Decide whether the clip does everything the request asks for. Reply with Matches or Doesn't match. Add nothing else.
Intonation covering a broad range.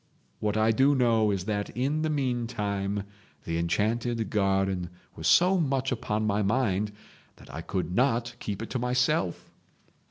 Doesn't match